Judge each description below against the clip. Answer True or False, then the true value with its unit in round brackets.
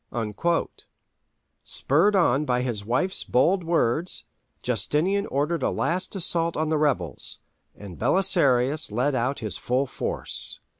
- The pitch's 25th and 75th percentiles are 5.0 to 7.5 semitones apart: True (5.6 semitones)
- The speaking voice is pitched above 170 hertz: False (145 Hz)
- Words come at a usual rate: False (130 wpm)